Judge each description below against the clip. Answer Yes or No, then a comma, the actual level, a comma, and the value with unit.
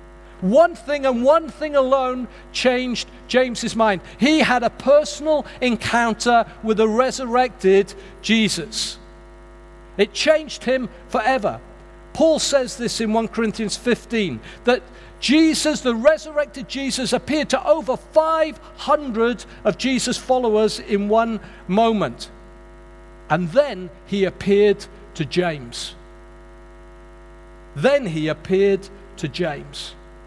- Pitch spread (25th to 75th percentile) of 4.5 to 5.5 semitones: Yes, average, 5.1 semitones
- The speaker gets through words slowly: Yes, slow, 110 wpm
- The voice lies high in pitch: Yes, high, 230 Hz